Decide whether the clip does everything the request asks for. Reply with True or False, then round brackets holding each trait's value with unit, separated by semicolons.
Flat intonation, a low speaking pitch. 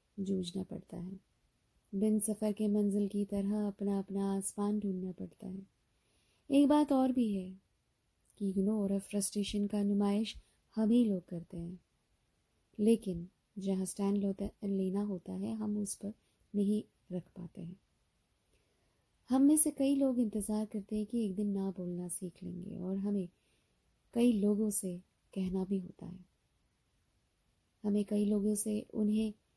False (1.9 semitones; 205 Hz)